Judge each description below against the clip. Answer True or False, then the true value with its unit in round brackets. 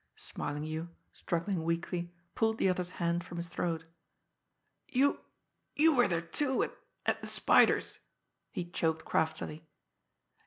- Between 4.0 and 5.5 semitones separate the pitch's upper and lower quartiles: False (2.9 semitones)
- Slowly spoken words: True (125 wpm)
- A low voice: False (170 Hz)